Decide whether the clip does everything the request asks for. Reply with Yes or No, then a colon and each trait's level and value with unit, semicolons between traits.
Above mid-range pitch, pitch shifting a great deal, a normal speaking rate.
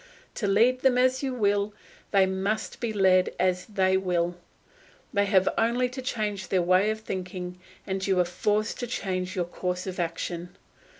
No: high, 195 Hz; average, 3.0 semitones; average, 175 wpm